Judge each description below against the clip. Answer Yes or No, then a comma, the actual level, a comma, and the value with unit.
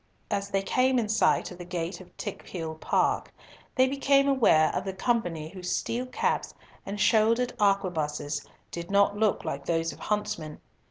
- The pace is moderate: Yes, average, 165 wpm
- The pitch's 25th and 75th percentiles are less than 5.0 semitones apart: No, wide, 5.4 semitones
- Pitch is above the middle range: Yes, high, 195 Hz